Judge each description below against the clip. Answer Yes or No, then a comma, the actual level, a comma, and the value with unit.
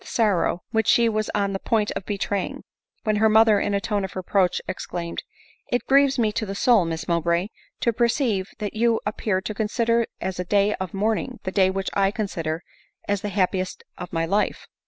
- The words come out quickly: Yes, fast, 215 wpm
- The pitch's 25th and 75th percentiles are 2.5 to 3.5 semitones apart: Yes, average, 2.8 semitones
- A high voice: Yes, high, 205 Hz